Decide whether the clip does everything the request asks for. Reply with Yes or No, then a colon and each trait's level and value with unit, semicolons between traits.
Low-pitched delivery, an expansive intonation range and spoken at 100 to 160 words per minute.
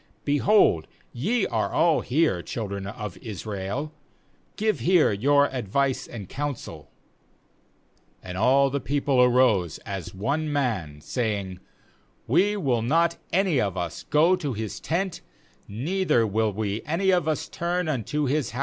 Yes: low, 130 Hz; wide, 7.2 semitones; average, 150 wpm